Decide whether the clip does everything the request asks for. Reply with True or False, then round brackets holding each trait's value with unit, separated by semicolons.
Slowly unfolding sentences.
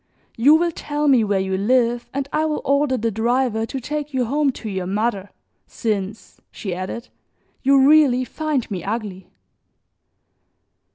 False (155 wpm)